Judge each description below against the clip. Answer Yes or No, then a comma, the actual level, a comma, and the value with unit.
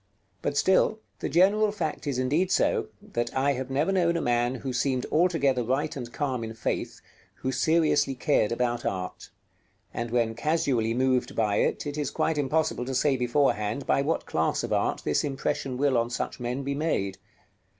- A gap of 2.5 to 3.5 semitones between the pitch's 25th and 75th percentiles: No, average, 4.0 semitones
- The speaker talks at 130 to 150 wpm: No, average, 180 wpm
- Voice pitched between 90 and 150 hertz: Yes, low, 135 Hz